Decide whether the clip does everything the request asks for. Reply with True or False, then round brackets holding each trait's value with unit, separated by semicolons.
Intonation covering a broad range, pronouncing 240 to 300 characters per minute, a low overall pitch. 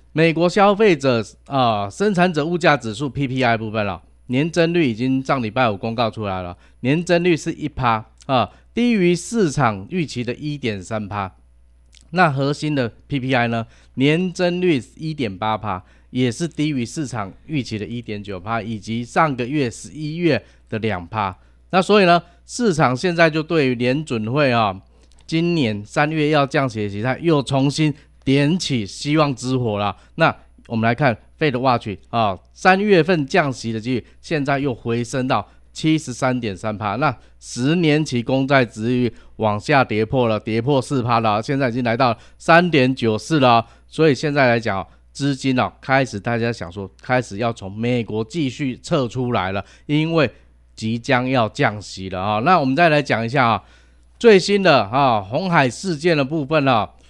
True (5.8 semitones; 255 characters per minute; 130 Hz)